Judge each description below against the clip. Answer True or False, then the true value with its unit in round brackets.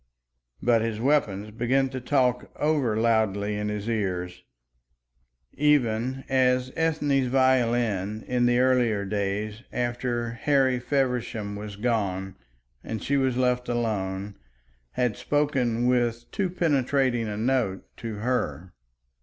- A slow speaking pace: True (120 wpm)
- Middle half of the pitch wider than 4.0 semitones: False (3.6 semitones)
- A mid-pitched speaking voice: False (120 Hz)